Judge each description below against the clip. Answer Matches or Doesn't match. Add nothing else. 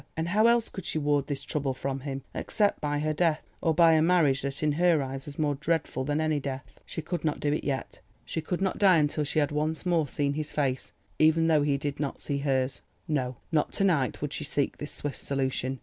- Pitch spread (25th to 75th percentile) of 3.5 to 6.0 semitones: Doesn't match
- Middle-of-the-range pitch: Matches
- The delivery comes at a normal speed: Doesn't match